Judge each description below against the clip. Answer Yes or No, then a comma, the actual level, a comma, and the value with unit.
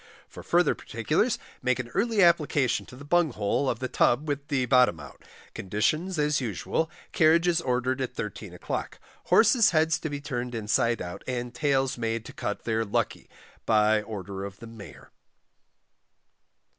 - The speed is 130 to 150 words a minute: No, average, 165 wpm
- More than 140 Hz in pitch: No, low, 125 Hz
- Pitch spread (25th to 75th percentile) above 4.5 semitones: Yes, average, 5.1 semitones